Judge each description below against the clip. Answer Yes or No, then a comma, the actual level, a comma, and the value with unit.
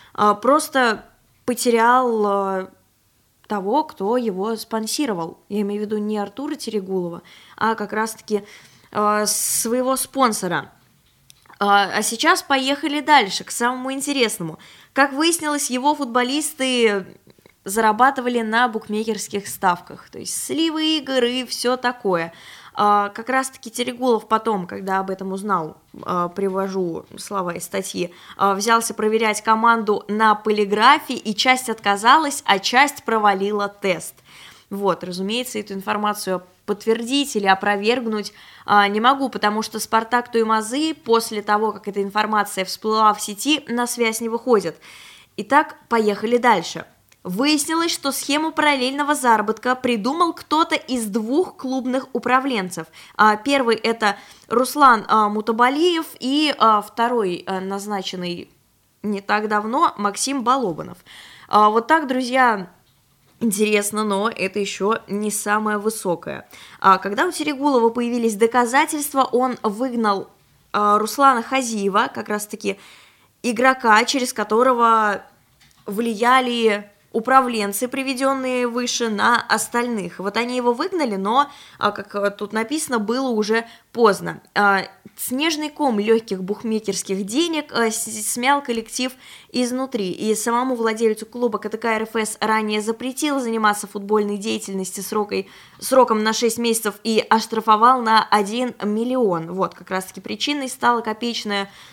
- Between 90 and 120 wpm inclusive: Yes, average, 115 wpm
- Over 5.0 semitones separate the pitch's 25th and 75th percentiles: No, average, 3.7 semitones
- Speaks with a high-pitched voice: Yes, high, 220 Hz